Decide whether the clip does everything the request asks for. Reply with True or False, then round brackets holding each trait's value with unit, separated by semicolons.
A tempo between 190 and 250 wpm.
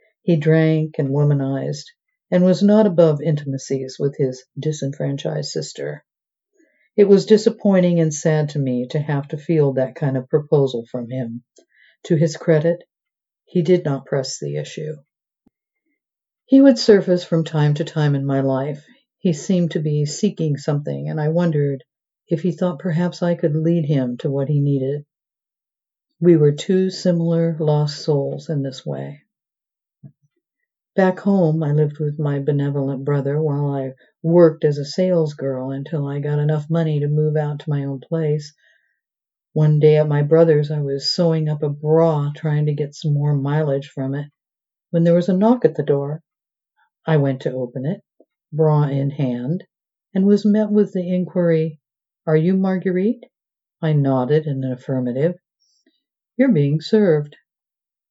False (165 wpm)